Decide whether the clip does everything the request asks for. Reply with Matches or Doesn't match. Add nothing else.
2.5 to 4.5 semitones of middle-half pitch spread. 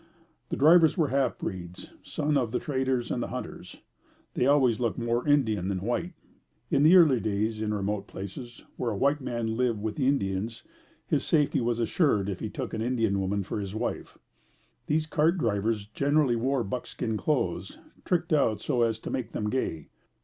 Doesn't match